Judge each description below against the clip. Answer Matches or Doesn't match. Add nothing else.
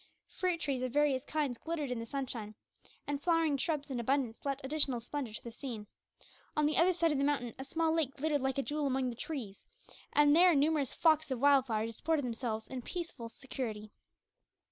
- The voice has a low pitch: Doesn't match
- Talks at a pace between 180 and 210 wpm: Matches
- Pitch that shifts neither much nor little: Matches